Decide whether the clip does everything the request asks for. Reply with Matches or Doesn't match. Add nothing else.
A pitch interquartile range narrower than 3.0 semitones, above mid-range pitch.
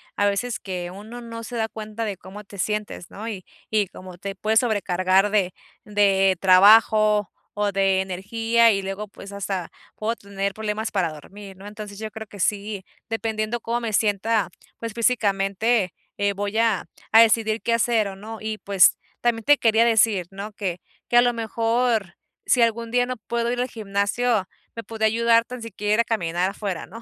Matches